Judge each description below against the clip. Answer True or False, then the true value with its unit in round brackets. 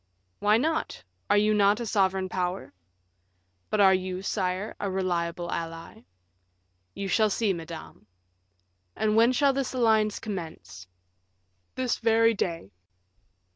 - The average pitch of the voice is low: False (200 Hz)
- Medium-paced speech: False (125 wpm)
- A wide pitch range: False (3.4 semitones)